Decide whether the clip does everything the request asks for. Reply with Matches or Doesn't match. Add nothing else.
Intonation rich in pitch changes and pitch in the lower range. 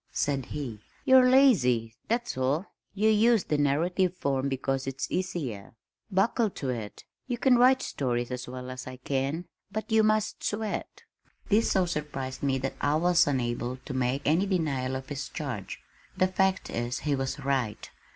Doesn't match